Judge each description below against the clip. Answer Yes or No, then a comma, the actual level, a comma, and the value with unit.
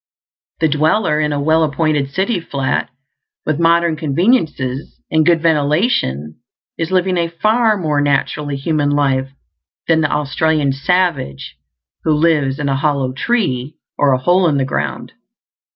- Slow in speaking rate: No, average, 145 wpm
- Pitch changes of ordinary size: Yes, average, 3.3 semitones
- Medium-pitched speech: Yes, medium, 155 Hz